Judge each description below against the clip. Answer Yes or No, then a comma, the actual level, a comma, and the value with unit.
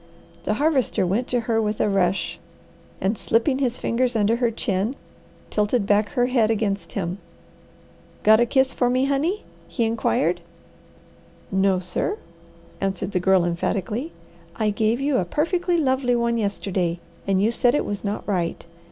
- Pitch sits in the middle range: No, high, 220 Hz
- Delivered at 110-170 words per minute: Yes, average, 160 wpm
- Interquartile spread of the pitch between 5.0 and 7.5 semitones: No, average, 4.3 semitones